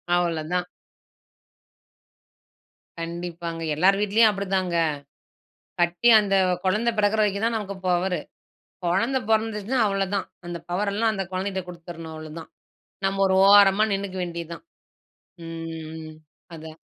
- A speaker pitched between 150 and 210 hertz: Yes, high, 190 Hz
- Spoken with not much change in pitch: No, average, 3.1 semitones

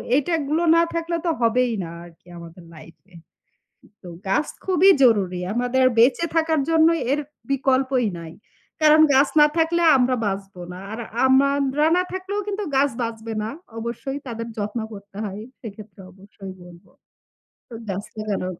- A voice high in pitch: Yes, high, 245 Hz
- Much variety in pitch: Yes, wide, 6.8 semitones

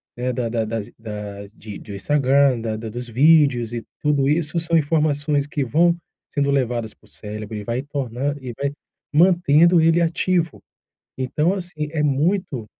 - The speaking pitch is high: No, medium, 140 Hz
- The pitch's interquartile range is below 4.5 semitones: No, average, 5.1 semitones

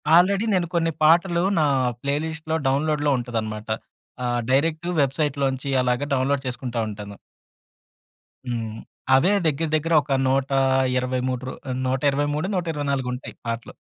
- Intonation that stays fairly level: No, average, 3.6 semitones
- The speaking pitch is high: No, low, 135 Hz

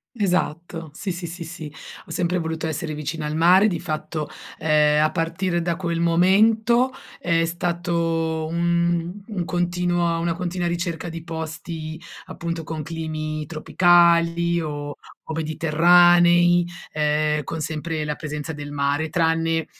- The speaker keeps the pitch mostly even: Yes, narrow, 1.8 semitones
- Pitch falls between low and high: Yes, medium, 165 Hz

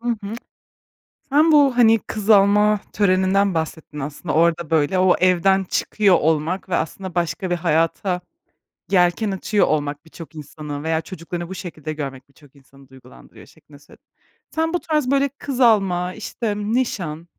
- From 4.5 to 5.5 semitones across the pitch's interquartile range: Yes, average, 4.8 semitones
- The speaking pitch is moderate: Yes, medium, 180 Hz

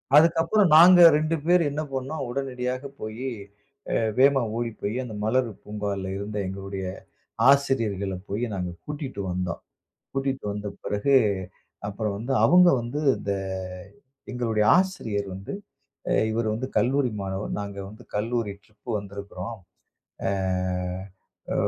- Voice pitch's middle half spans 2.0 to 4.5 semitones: No, average, 5.2 semitones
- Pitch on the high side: No, low, 115 Hz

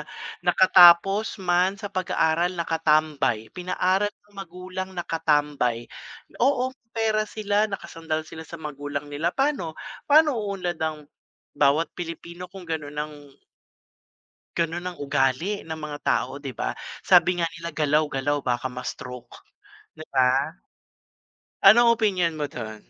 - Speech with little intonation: No, average, 4.3 semitones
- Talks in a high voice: No, medium, 165 Hz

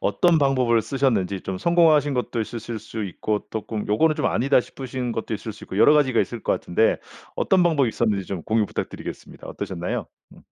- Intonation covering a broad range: No, average, 4.6 semitones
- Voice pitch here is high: No, low, 115 Hz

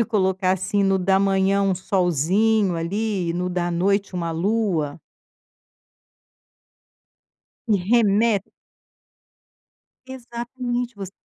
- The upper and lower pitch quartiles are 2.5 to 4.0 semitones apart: Yes, average, 3.3 semitones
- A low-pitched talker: No, high, 195 Hz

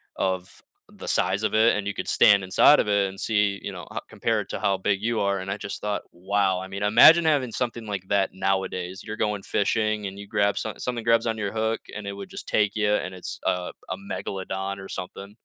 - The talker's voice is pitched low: Yes, low, 100 Hz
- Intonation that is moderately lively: No, narrow, 2.1 semitones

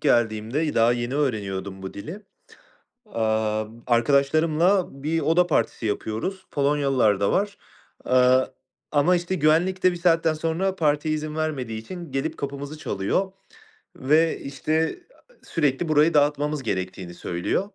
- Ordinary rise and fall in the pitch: No, wide, 6.1 semitones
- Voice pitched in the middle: Yes, medium, 145 Hz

